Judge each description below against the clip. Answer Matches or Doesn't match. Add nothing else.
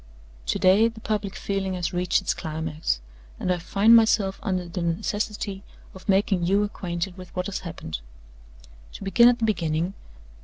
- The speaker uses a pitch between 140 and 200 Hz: Matches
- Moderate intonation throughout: Matches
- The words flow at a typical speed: Matches